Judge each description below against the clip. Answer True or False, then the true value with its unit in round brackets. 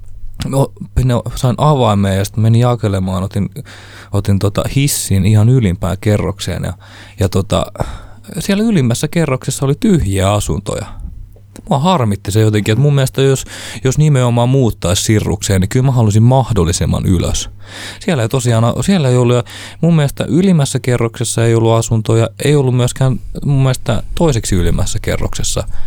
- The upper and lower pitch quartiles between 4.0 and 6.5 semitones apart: True (4.7 semitones)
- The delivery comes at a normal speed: True (140 wpm)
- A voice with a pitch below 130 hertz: True (110 Hz)